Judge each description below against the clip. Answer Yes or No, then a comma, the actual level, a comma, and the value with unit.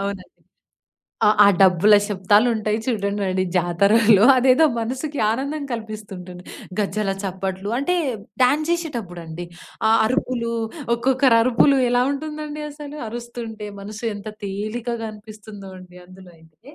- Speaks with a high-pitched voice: Yes, high, 215 Hz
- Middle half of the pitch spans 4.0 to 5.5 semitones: Yes, average, 4.5 semitones